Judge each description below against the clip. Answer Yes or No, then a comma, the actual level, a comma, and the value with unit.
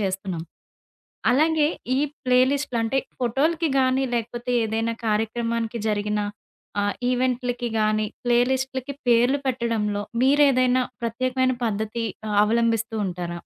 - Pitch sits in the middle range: No, high, 235 Hz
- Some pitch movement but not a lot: Yes, average, 3.0 semitones